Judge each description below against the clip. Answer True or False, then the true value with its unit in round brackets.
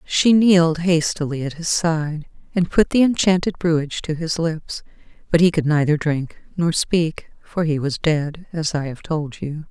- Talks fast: False (185 wpm)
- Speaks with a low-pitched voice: False (160 Hz)